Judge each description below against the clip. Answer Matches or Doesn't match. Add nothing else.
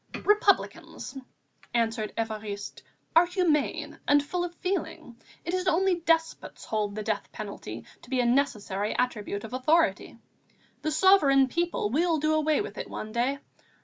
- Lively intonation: Matches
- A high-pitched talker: Matches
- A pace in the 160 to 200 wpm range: Doesn't match